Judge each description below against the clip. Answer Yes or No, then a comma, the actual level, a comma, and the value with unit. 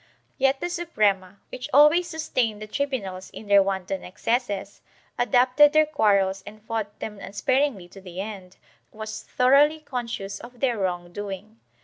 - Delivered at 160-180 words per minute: No, average, 150 wpm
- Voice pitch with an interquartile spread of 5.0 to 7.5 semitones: Yes, wide, 5.4 semitones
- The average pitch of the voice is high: Yes, high, 215 Hz